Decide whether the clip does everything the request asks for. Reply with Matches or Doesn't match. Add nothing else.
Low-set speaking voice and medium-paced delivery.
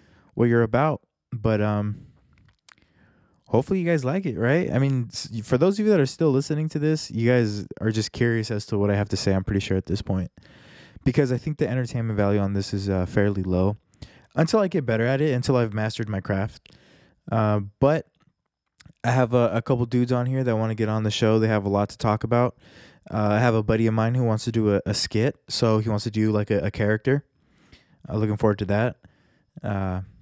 Doesn't match